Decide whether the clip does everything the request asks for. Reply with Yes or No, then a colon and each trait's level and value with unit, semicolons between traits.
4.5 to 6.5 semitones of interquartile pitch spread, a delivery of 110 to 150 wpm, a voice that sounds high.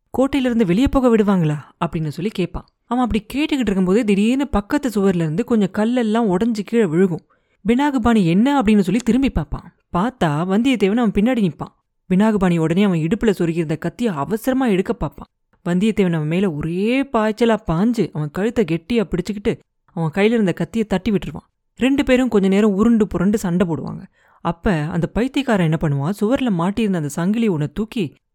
Yes: average, 5.1 semitones; average, 125 wpm; high, 205 Hz